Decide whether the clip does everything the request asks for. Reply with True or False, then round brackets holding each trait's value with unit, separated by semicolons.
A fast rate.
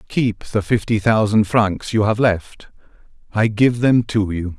False (155 wpm)